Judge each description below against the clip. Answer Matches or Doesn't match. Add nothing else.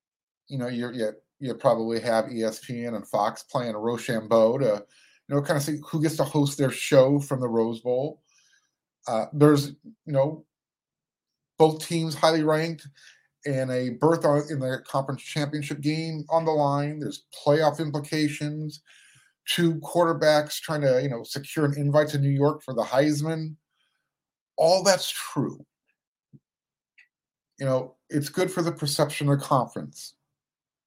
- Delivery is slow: Doesn't match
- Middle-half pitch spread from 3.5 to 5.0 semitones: Doesn't match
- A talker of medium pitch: Matches